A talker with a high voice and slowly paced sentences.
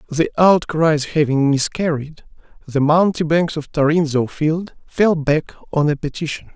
No: medium, 155 Hz; slow, 130 wpm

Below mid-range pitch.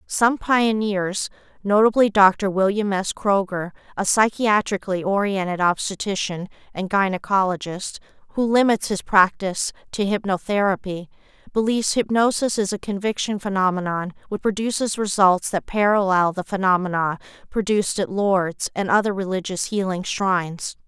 No: high, 195 Hz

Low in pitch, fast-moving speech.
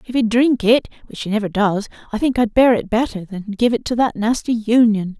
No: high, 225 Hz; fast, 245 wpm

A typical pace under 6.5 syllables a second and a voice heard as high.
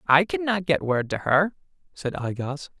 No: 4.5 syllables/s; medium, 155 Hz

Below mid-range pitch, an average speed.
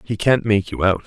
No: low, 105 Hz; fast, 280 wpm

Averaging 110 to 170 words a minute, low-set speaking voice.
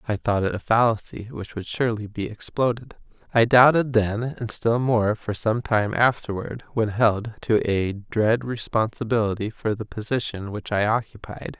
Yes: average, 165 wpm; low, 110 Hz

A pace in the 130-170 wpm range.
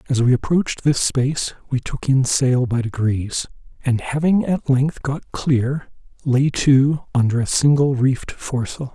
Yes: average, 160 wpm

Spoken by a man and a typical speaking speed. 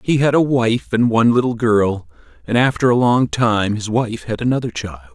No: male; fast, 210 wpm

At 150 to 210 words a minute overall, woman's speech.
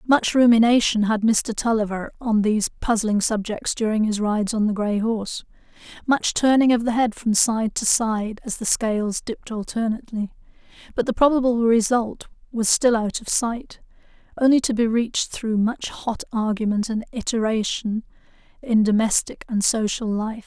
Yes: average, 160 wpm; female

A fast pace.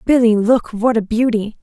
No: average, 185 wpm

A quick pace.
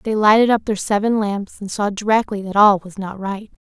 Yes: fast, 230 wpm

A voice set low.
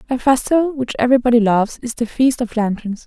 No: high, 240 Hz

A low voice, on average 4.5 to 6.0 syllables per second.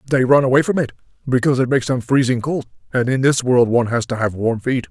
No: low, 130 Hz; 6.5 syllables/s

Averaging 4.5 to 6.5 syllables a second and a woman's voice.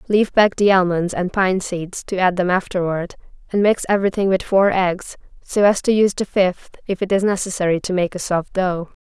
Yes: 5.3 syllables/s; female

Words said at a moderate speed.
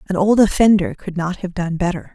No: fast, 225 wpm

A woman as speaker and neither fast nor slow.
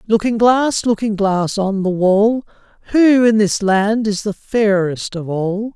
No: male; average, 165 wpm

